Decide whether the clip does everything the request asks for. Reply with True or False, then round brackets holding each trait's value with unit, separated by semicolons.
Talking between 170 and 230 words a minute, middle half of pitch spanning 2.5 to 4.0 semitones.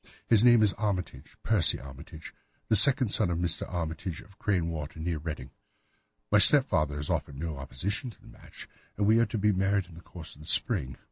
False (195 wpm; 5.0 semitones)